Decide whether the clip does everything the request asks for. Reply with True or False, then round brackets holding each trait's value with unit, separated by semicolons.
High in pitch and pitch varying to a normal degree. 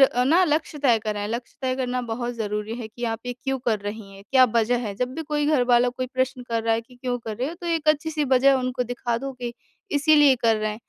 True (245 Hz; 3.1 semitones)